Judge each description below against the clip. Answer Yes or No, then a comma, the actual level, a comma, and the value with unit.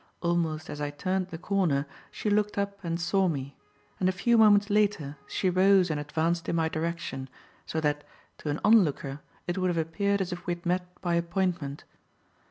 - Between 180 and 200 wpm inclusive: Yes, average, 190 wpm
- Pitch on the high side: No, medium, 175 Hz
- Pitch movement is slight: No, average, 3.5 semitones